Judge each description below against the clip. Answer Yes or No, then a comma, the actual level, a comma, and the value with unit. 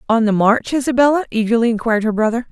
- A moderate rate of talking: Yes, average, 190 wpm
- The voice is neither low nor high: No, high, 235 Hz